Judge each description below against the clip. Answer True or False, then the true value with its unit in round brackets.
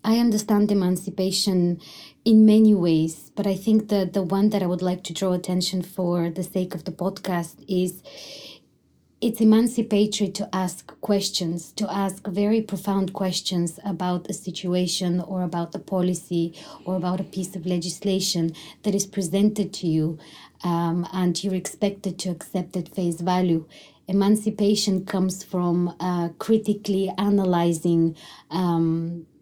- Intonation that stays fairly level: True (2.3 semitones)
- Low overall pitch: False (185 Hz)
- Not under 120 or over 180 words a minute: True (145 wpm)